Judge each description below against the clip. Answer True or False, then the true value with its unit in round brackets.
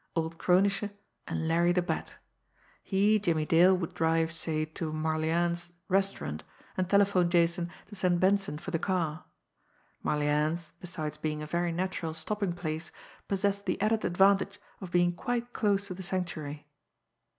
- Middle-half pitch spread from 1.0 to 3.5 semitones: True (3.1 semitones)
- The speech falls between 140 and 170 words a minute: True (150 wpm)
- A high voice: False (175 Hz)